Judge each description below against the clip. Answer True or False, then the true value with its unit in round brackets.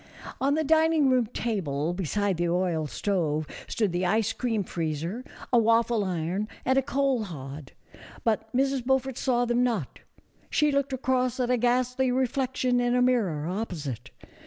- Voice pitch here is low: False (230 Hz)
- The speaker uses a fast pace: False (160 wpm)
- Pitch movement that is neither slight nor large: False (6.3 semitones)